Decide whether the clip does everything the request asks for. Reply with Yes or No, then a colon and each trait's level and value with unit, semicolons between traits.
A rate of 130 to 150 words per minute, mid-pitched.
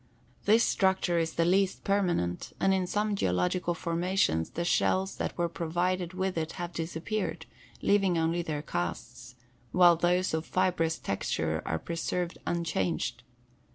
Yes: average, 140 wpm; medium, 170 Hz